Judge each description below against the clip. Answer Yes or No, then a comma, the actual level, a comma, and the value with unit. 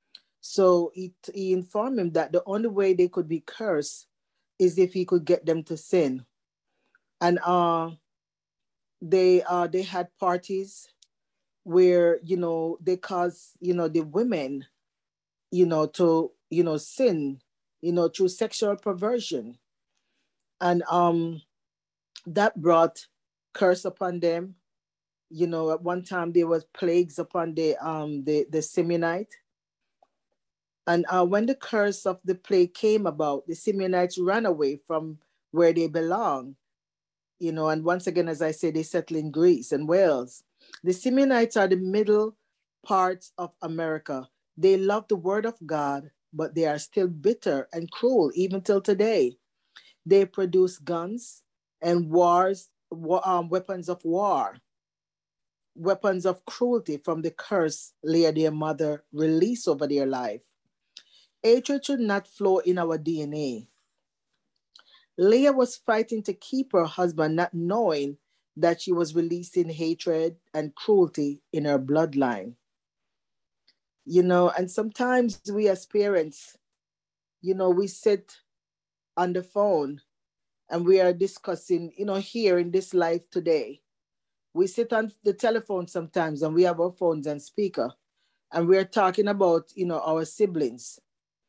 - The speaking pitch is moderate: Yes, medium, 175 Hz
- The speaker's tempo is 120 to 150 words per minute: Yes, average, 145 wpm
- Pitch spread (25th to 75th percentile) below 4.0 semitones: Yes, average, 3.1 semitones